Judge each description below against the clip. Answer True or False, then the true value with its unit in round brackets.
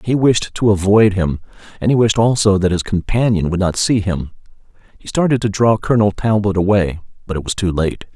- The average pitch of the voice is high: False (100 Hz)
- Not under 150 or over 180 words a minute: False (205 wpm)